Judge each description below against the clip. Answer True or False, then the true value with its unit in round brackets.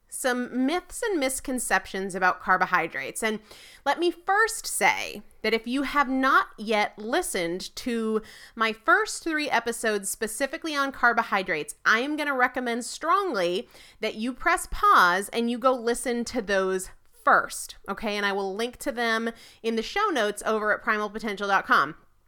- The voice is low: False (235 Hz)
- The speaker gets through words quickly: False (155 wpm)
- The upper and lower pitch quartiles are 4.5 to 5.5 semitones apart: True (4.9 semitones)